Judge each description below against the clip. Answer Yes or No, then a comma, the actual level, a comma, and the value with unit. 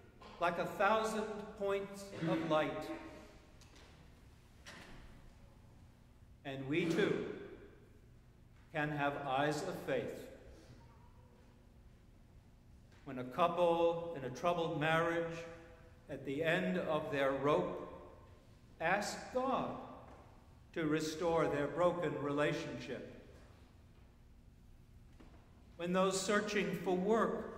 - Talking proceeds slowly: Yes, slow, 85 wpm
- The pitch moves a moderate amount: Yes, average, 4.8 semitones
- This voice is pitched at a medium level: Yes, medium, 165 Hz